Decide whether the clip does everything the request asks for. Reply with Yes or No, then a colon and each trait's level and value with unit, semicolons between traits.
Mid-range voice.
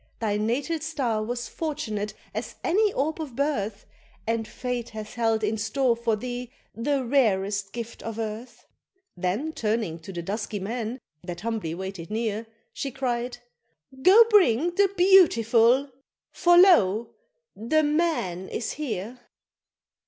No: high, 230 Hz